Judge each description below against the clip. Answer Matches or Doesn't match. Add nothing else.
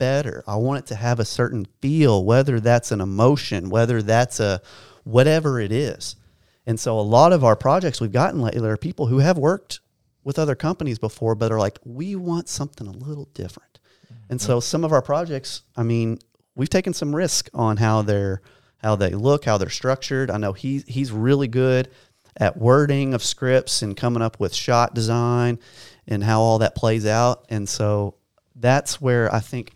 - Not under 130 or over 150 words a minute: Doesn't match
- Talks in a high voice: Doesn't match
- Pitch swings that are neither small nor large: Matches